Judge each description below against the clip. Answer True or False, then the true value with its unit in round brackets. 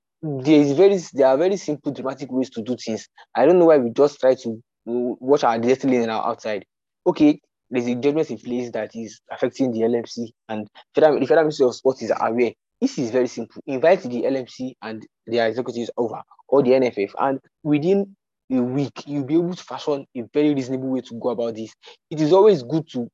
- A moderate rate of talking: False (210 wpm)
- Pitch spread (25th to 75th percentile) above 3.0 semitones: True (4.0 semitones)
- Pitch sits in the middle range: False (130 Hz)